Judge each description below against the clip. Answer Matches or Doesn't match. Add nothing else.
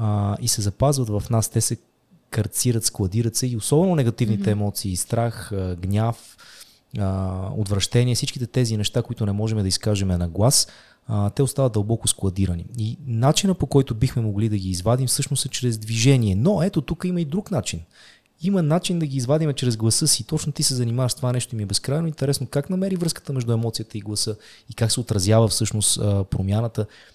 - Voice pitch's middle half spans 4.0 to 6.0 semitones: Matches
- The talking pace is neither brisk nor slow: Doesn't match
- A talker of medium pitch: Doesn't match